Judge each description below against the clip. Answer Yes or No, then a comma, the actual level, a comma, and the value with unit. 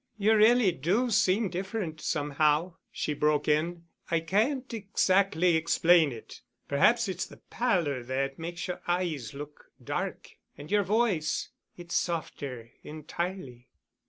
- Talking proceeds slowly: Yes, slow, 120 wpm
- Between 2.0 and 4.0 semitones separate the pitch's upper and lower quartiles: No, average, 4.8 semitones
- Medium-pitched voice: Yes, medium, 170 Hz